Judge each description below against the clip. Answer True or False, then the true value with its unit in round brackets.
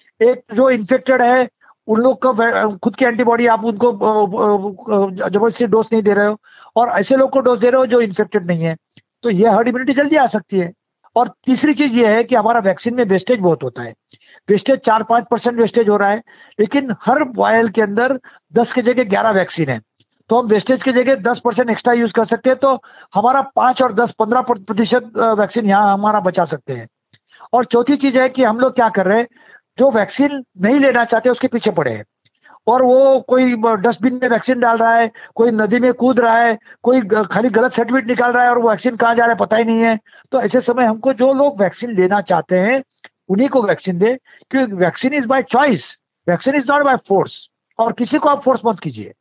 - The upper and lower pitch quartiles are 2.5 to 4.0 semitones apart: True (3.0 semitones)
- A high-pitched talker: True (235 Hz)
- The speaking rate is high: True (220 wpm)